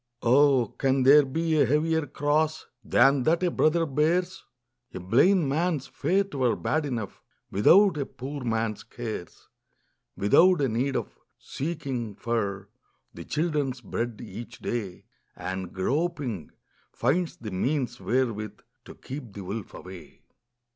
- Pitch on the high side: No, low, 135 Hz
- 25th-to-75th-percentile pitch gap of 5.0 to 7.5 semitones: Yes, wide, 5.4 semitones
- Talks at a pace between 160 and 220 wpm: No, slow, 135 wpm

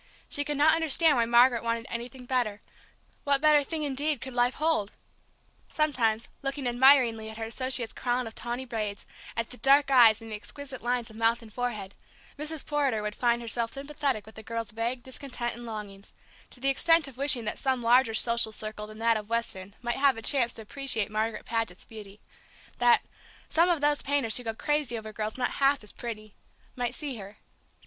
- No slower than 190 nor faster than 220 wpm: Yes, average, 195 wpm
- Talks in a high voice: Yes, high, 240 Hz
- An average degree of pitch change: Yes, average, 3.7 semitones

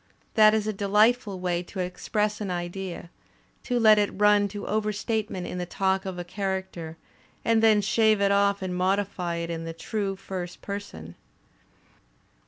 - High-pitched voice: Yes, high, 195 Hz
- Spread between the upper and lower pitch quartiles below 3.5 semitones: Yes, average, 2.7 semitones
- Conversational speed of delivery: Yes, average, 165 wpm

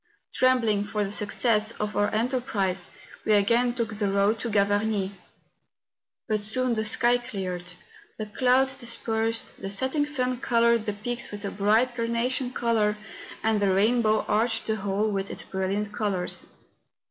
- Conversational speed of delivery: Yes, average, 155 wpm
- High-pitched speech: Yes, high, 220 Hz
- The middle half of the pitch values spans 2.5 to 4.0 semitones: Yes, average, 2.8 semitones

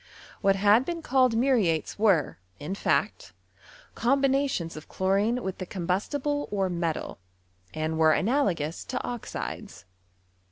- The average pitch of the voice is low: No, high, 200 Hz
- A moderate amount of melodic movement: No, wide, 7.1 semitones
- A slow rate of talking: Yes, slow, 120 wpm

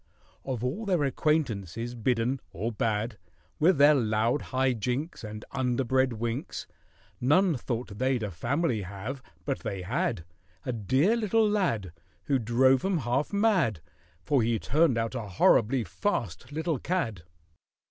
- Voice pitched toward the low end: Yes, low, 125 Hz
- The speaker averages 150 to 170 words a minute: No, slow, 135 wpm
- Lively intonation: No, average, 4.8 semitones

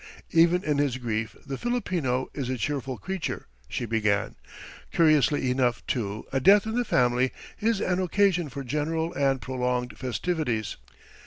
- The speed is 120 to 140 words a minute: No, average, 150 wpm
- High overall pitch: No, low, 135 Hz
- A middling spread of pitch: No, wide, 5.7 semitones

